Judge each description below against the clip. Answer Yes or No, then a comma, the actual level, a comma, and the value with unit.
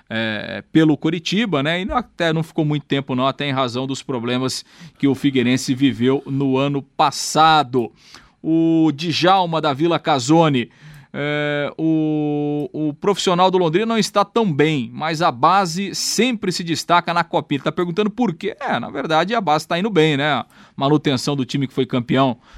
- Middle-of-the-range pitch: Yes, medium, 155 Hz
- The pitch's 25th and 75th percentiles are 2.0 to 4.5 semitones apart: Yes, average, 3.8 semitones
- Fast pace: No, average, 175 wpm